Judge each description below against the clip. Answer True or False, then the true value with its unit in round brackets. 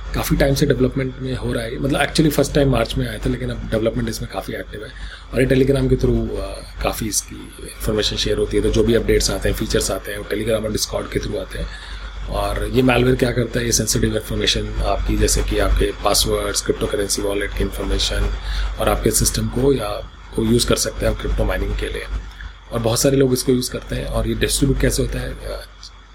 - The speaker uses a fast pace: True (225 wpm)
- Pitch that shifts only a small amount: False (3.7 semitones)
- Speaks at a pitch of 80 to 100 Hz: False (115 Hz)